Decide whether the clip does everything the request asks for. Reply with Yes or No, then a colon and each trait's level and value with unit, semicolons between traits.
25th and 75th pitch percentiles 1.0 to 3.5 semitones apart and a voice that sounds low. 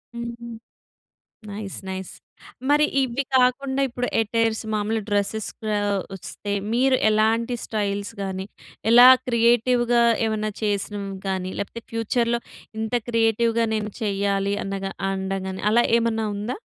No: average, 2.7 semitones; high, 220 Hz